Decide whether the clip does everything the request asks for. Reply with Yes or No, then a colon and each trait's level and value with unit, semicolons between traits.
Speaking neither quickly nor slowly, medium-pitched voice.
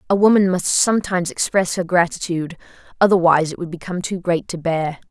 Yes: average, 165 wpm; medium, 175 Hz